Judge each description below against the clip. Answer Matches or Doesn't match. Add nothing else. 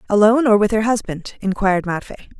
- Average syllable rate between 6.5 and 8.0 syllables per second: Matches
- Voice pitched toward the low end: Doesn't match